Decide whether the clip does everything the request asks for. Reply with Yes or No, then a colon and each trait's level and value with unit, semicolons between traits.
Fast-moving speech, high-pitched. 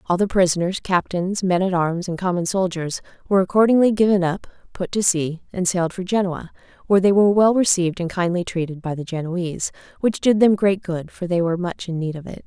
No: fast, 215 wpm; medium, 180 Hz